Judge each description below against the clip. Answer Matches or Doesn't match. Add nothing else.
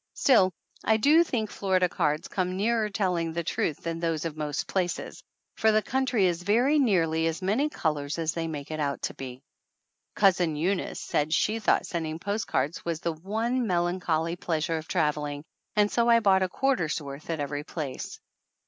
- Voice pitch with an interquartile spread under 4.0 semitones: Doesn't match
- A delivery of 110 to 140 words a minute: Doesn't match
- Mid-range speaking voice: Matches